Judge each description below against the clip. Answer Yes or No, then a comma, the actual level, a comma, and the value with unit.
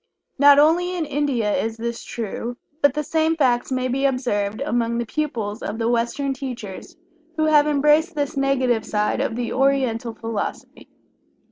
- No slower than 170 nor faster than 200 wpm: No, average, 160 wpm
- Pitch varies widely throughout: No, average, 4.0 semitones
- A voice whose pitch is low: No, very high, 255 Hz